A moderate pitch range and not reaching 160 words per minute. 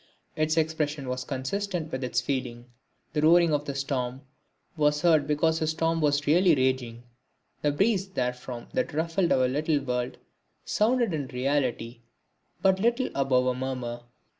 Yes: average, 4.2 semitones; average, 150 wpm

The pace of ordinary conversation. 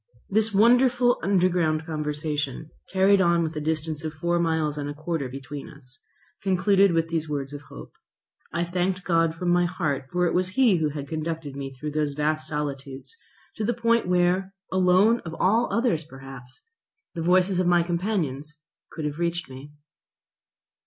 Yes: average, 170 wpm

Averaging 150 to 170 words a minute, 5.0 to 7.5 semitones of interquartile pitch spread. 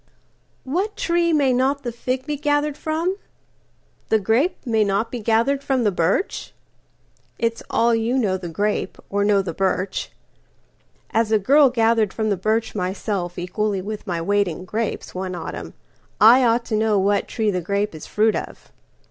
No: average, 155 wpm; average, 4.4 semitones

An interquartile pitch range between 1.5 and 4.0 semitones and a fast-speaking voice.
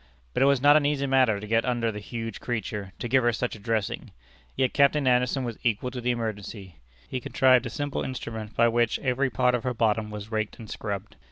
Yes: average, 2.8 semitones; fast, 230 wpm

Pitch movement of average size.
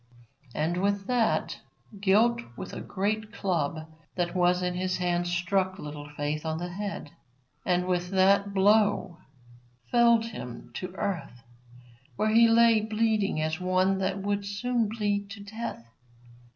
Yes: average, 3.3 semitones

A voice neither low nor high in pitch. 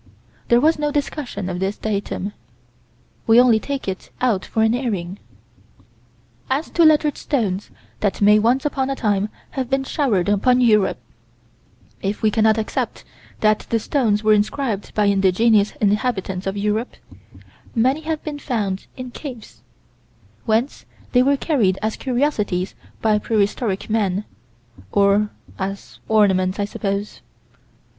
No: high, 215 Hz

